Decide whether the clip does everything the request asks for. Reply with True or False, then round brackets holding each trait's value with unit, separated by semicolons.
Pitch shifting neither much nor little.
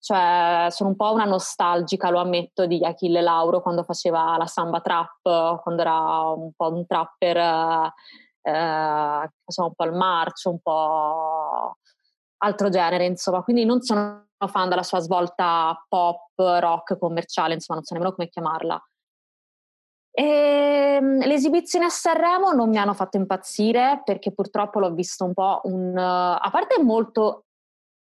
True (3.2 semitones)